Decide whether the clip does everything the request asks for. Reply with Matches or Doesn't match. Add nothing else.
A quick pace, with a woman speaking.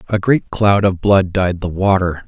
Doesn't match